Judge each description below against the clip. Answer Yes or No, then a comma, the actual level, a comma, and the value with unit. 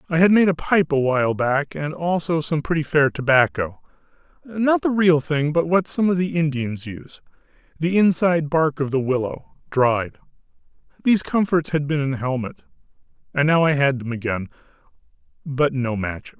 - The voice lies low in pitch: No, medium, 150 Hz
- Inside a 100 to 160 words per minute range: No, average, 175 wpm